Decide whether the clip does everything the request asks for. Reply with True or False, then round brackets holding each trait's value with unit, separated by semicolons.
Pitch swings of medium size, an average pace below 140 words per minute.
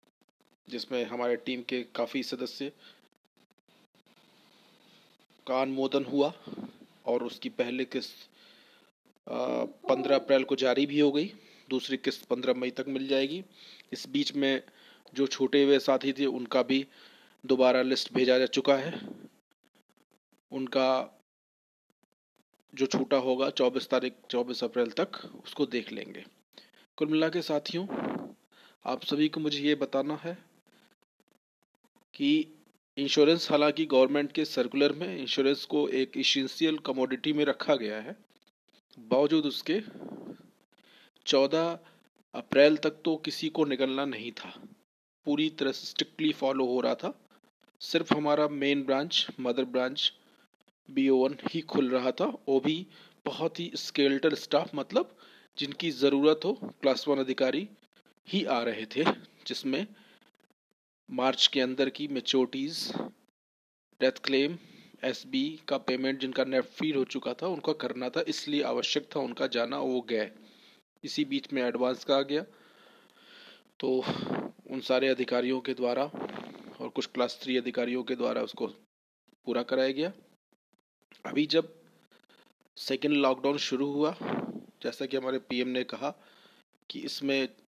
True (3.2 semitones; 130 wpm)